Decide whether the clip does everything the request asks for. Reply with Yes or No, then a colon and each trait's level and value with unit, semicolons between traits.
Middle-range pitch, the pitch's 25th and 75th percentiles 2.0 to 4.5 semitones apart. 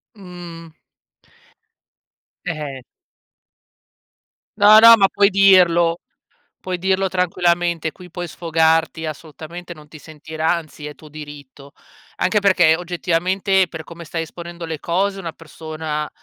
Yes: medium, 170 Hz; narrow, 2.6 semitones